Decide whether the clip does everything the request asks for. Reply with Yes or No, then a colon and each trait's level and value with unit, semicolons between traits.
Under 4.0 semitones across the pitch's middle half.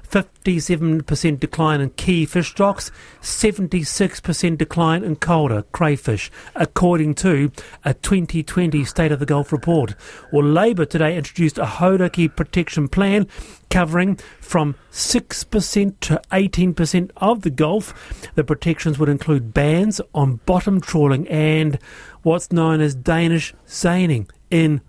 Yes: average, 3.2 semitones